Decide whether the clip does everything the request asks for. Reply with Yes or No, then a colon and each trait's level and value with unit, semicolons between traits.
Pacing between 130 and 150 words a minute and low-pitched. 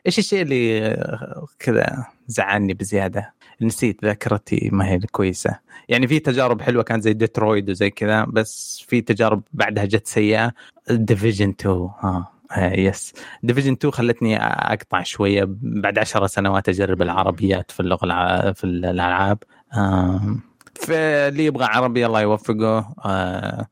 Yes: fast, 135 wpm; low, 105 Hz